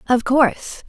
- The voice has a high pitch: Yes, very high, 255 Hz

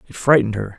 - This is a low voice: Yes, low, 115 Hz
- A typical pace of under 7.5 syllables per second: No, 7.7 syllables/s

